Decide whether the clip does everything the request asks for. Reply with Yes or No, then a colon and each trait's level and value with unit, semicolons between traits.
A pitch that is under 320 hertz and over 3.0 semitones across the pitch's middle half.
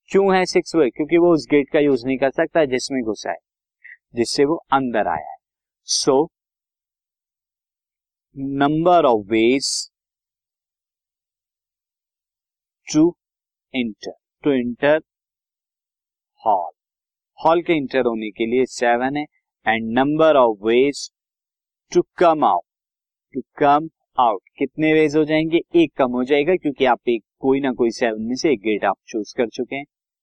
Yes: medium, 140 Hz; average, 4.3 semitones